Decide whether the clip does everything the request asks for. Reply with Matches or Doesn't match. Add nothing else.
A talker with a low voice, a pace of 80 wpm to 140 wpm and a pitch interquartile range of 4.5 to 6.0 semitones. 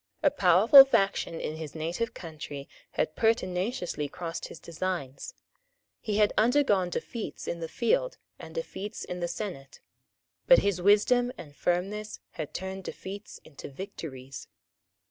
Doesn't match